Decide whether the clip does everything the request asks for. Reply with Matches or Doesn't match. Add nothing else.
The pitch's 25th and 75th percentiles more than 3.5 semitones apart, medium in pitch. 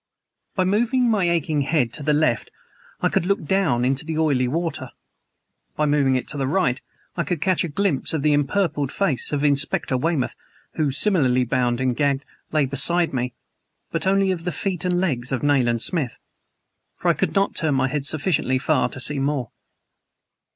Matches